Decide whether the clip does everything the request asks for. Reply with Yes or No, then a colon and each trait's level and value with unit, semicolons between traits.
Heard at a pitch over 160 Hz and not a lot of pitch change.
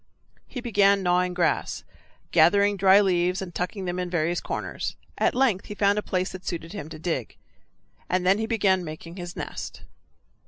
Yes: medium, 185 Hz; narrow, 2.3 semitones